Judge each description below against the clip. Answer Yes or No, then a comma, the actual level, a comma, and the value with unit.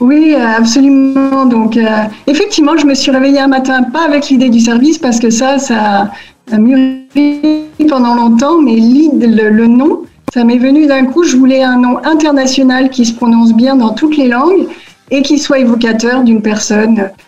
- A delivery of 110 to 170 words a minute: No, average, 185 wpm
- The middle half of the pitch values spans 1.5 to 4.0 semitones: Yes, average, 3.5 semitones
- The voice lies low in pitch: No, very high, 260 Hz